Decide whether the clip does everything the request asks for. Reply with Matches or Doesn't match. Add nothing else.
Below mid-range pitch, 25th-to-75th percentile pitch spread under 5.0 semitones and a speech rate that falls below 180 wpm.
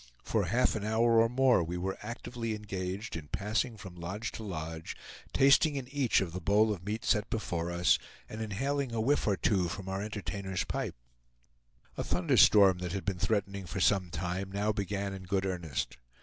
Doesn't match